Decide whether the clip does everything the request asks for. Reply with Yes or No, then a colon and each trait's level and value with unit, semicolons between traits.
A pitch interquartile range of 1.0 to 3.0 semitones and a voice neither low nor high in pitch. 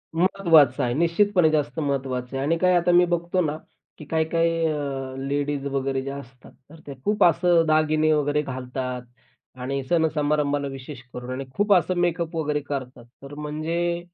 No: average, 3.6 semitones; medium, 150 Hz